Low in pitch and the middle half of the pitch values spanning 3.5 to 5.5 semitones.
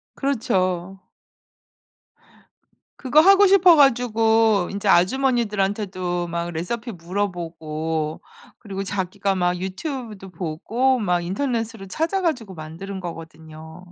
No: high, 195 Hz; average, 5.2 semitones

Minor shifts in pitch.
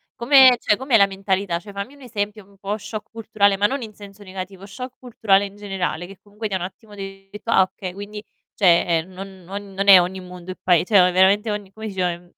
Yes: narrow, 1.9 semitones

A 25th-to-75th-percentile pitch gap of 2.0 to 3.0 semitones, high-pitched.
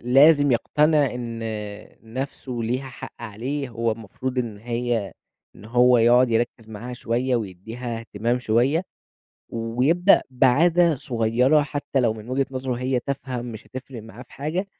No: average, 2.7 semitones; low, 125 Hz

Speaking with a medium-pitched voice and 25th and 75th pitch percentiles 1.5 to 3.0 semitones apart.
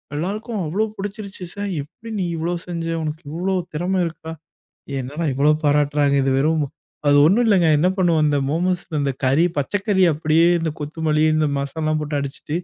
No: medium, 160 Hz; average, 3.8 semitones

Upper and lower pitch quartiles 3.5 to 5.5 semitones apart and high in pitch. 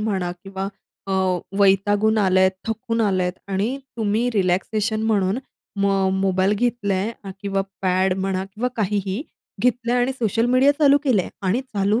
No: average, 3.0 semitones; high, 205 Hz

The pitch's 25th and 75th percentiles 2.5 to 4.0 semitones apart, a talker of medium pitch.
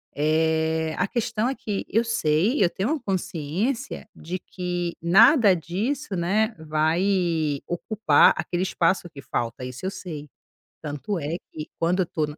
No: average, 4.5 semitones; medium, 175 Hz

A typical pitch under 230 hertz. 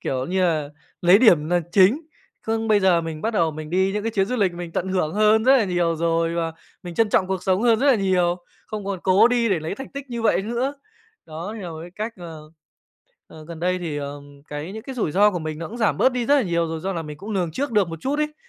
Yes: medium, 185 Hz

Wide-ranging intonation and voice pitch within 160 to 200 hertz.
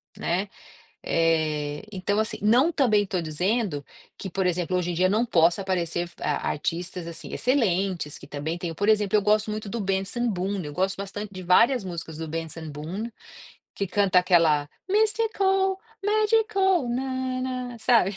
Yes: wide, 5.8 semitones; high, 195 Hz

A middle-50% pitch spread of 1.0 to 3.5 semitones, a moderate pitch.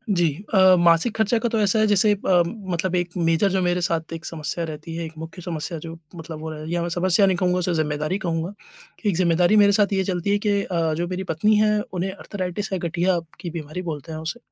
Yes: average, 2.8 semitones; medium, 175 Hz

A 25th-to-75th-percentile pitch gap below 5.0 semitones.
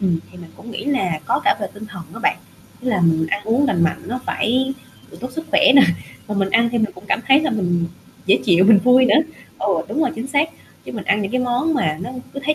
No: wide, 5.4 semitones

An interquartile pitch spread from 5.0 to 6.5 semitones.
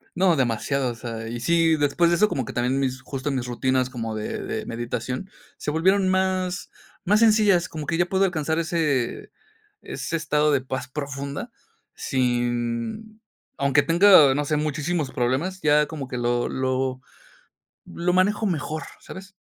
Yes: wide, 5.4 semitones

